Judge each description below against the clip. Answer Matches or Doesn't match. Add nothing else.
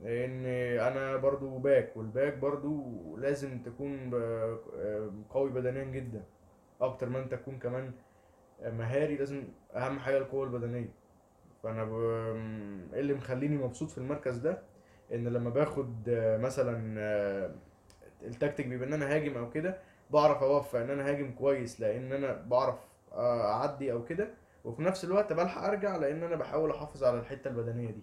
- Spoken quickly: Matches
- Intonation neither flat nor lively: Matches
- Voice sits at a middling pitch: Doesn't match